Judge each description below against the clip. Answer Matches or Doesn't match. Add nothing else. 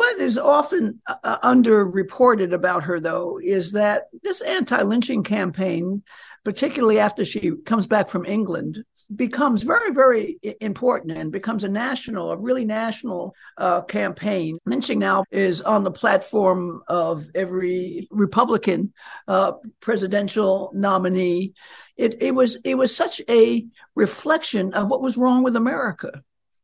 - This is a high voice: Matches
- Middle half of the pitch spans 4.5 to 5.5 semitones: Matches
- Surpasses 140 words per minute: Doesn't match